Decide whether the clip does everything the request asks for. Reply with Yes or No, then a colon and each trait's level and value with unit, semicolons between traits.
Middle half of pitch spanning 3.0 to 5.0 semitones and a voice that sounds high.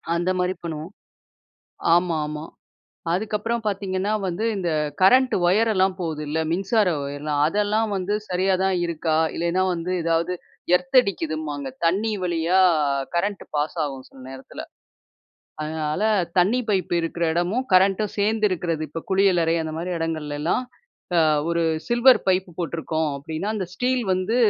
No: average, 3.8 semitones; medium, 180 Hz